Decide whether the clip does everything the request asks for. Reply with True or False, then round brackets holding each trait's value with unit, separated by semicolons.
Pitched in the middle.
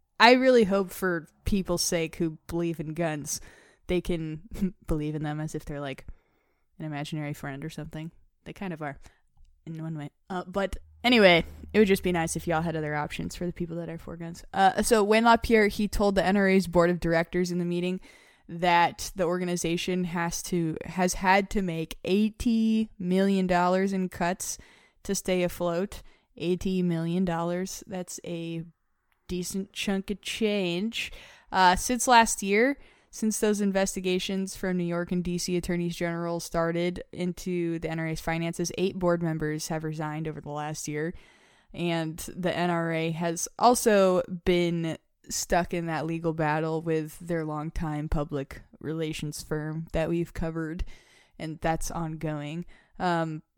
True (175 Hz)